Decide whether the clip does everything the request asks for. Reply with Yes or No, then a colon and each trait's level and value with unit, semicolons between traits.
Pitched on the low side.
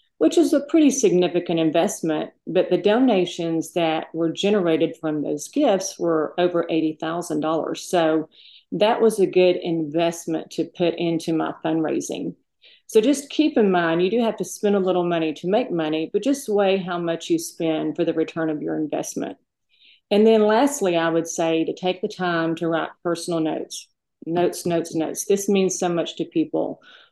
No: medium, 170 Hz